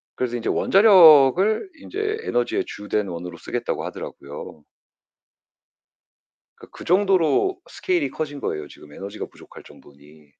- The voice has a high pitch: No, low, 135 Hz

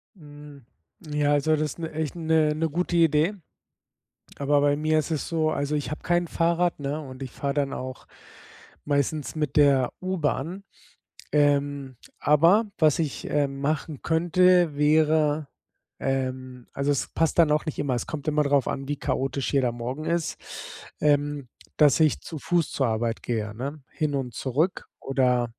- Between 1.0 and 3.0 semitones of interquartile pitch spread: Yes, narrow, 2.4 semitones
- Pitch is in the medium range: Yes, medium, 145 Hz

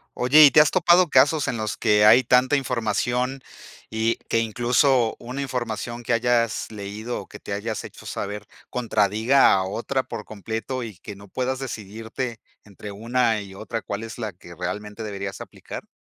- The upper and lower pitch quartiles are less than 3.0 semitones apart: No, average, 3.3 semitones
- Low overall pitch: Yes, low, 115 Hz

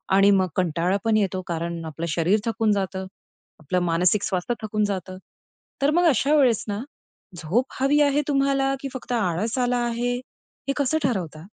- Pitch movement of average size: No, wide, 6.1 semitones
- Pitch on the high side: Yes, high, 205 Hz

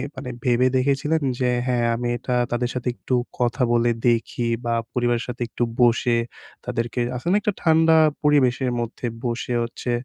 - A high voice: No, low, 125 Hz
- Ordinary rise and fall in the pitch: No, narrow, 1.7 semitones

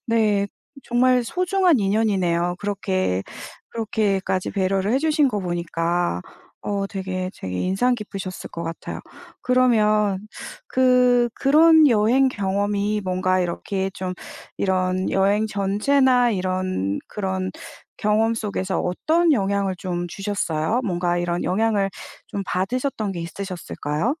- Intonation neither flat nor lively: Yes, average, 3.7 semitones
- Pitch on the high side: Yes, high, 200 Hz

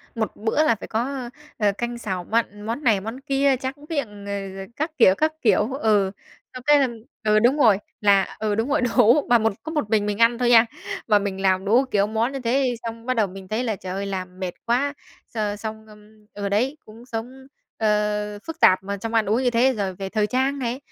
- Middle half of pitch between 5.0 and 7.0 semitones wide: No, average, 3.7 semitones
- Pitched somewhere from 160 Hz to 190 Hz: No, high, 225 Hz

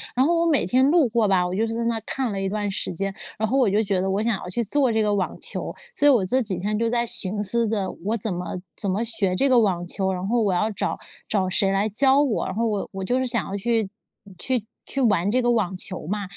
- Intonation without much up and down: No, average, 3.6 semitones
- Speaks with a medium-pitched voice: No, high, 215 Hz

